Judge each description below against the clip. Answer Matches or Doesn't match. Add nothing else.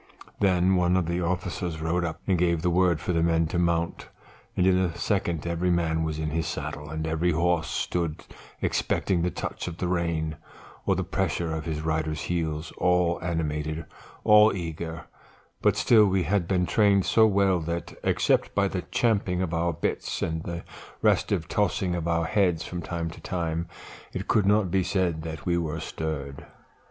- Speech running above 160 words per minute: Matches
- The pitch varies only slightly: Matches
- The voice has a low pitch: Matches